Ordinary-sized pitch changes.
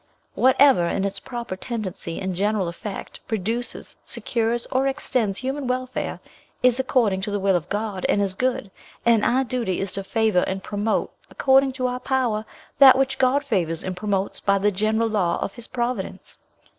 Yes: average, 4.5 semitones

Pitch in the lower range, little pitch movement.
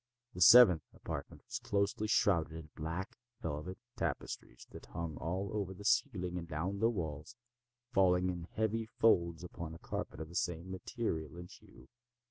No: very low, 90 Hz; average, 3.5 semitones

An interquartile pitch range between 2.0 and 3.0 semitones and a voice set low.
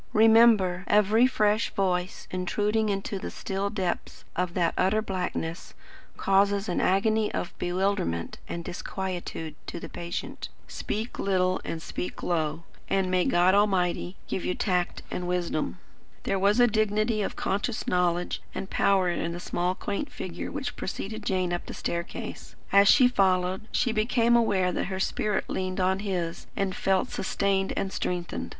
No: narrow, 2.6 semitones; high, 190 Hz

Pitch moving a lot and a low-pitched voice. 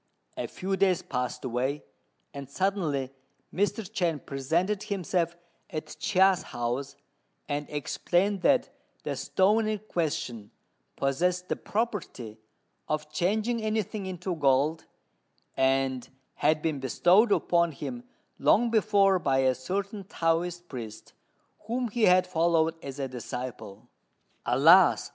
No: wide, 6.3 semitones; medium, 170 Hz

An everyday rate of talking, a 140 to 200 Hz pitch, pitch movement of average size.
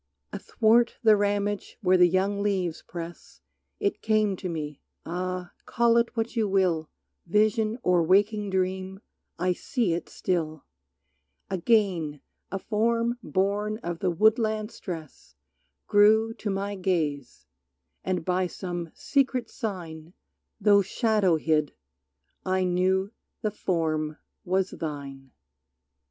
No: slow, 120 wpm; high, 190 Hz; average, 3.7 semitones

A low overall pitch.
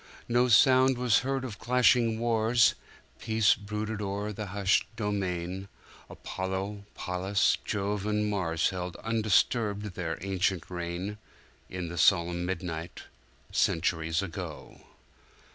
Yes: low, 100 Hz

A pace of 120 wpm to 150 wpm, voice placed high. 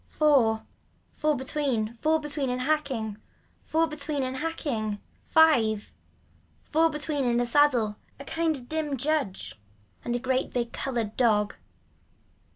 Yes: average, 140 wpm; very high, 265 Hz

